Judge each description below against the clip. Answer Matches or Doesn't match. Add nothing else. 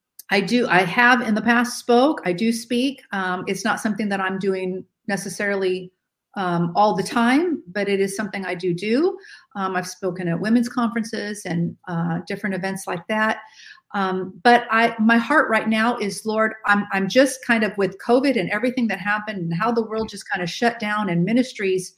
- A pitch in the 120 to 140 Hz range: Doesn't match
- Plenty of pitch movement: Doesn't match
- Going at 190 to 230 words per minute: Matches